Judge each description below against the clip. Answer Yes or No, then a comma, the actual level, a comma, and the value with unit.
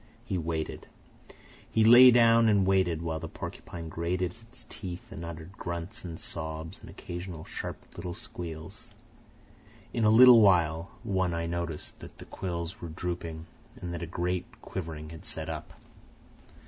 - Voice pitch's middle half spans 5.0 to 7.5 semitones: No, average, 2.7 semitones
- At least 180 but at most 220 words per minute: No, average, 155 wpm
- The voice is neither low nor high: No, very low, 85 Hz